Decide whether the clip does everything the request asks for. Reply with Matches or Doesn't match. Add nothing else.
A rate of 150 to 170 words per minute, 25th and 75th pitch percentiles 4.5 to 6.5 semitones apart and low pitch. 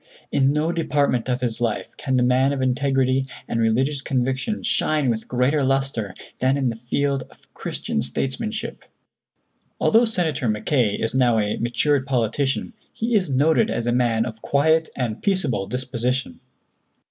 Doesn't match